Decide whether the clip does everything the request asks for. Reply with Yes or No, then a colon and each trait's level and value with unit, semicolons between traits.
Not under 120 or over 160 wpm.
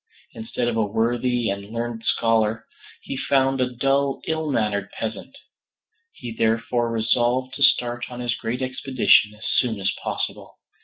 Yes: average, 150 wpm